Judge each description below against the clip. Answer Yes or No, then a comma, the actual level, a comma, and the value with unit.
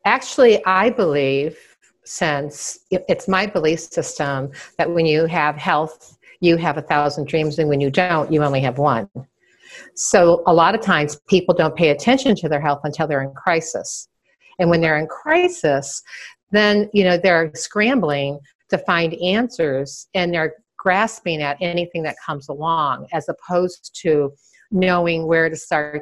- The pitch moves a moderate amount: Yes, average, 3.6 semitones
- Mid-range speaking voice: Yes, medium, 165 Hz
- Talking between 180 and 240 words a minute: No, average, 160 wpm